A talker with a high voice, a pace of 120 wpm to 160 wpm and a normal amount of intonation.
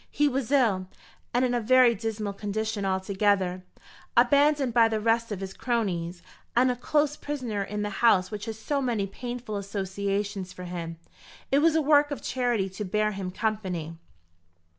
No: high, 215 Hz; average, 170 wpm; average, 4.2 semitones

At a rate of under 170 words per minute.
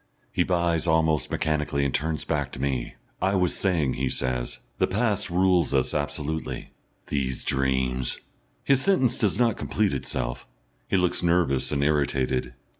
Yes: average, 155 wpm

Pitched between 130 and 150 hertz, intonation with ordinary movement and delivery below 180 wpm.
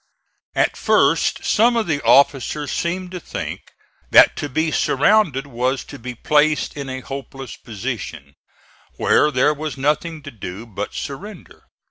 Yes: medium, 140 Hz; average, 3.5 semitones; average, 145 wpm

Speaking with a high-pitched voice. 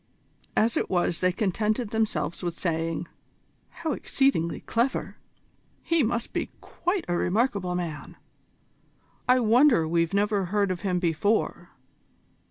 Yes: high, 200 Hz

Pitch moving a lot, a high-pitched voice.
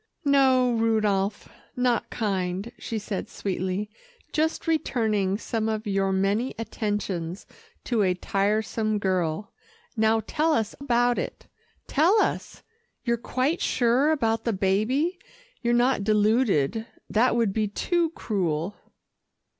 No: average, 3.8 semitones; high, 220 Hz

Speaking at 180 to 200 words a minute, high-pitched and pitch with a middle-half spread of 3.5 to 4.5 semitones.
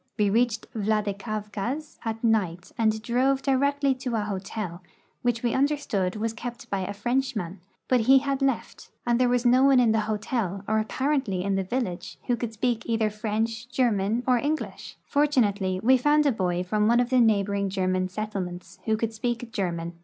Yes: average, 185 wpm; high, 225 Hz; average, 3.8 semitones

